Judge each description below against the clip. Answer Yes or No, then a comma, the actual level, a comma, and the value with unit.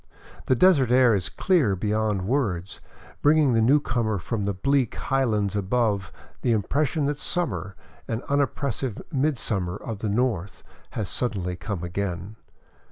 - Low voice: Yes, low, 110 Hz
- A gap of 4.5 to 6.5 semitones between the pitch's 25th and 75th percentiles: Yes, average, 5.2 semitones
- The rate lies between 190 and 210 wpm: No, average, 140 wpm